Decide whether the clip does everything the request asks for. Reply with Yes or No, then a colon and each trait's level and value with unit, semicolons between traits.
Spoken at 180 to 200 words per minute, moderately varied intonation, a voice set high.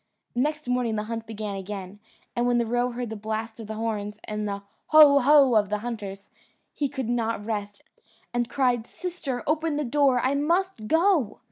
Yes: average, 190 wpm; average, 4.7 semitones; high, 235 Hz